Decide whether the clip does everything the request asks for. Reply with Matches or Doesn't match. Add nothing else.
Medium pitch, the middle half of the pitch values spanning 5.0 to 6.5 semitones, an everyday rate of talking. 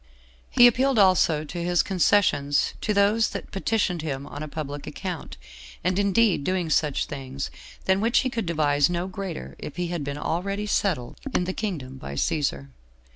Matches